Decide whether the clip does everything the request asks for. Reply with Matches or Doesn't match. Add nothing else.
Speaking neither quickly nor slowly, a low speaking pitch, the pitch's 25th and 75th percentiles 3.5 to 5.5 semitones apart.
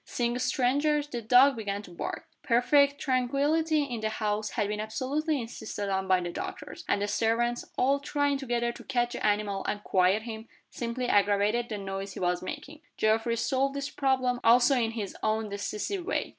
Doesn't match